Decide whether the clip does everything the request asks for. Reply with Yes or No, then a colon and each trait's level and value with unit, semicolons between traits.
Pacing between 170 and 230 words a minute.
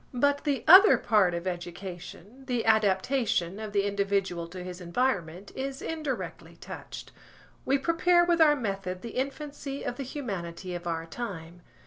No: average, 150 wpm